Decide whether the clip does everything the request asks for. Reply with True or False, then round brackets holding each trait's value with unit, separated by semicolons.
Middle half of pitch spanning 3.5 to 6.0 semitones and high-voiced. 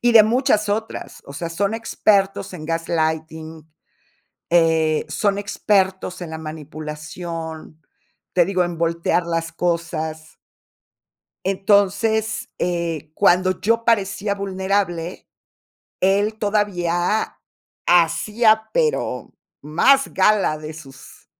False (4.0 semitones; 180 Hz)